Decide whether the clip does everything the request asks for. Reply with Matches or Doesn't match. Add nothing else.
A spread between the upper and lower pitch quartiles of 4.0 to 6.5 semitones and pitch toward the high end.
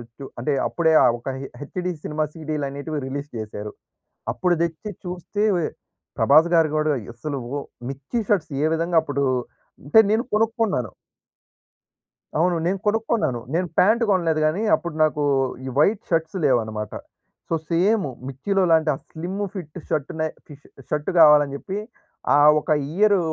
Doesn't match